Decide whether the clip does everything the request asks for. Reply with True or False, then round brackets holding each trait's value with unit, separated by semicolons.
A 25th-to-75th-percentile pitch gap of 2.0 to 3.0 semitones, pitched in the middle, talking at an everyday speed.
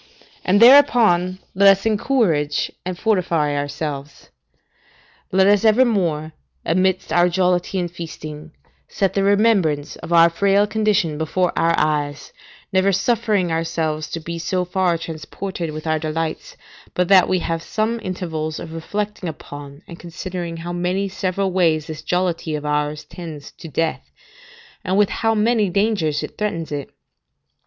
False (3.8 semitones; 175 Hz; 145 wpm)